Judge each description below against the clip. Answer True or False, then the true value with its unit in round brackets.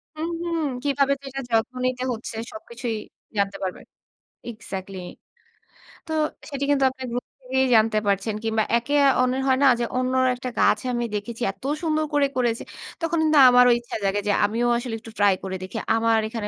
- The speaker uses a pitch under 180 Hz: False (240 Hz)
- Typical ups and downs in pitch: True (3.5 semitones)